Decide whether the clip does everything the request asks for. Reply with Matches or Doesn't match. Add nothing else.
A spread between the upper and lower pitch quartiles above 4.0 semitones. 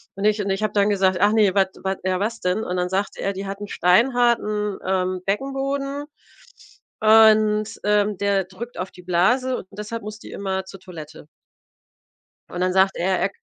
Doesn't match